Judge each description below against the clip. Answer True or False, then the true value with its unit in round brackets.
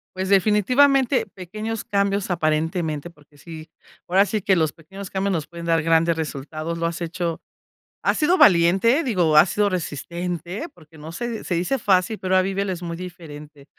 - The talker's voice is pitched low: False (175 Hz)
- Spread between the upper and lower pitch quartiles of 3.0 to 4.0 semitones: True (3.5 semitones)